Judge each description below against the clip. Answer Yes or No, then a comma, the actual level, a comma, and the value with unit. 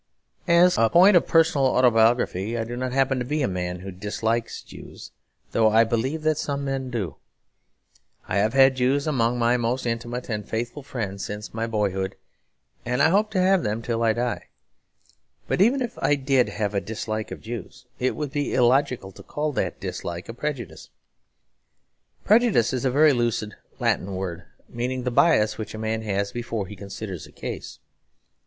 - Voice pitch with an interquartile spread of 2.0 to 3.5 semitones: No, average, 4.1 semitones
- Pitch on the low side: Yes, low, 120 Hz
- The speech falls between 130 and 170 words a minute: No, average, 180 wpm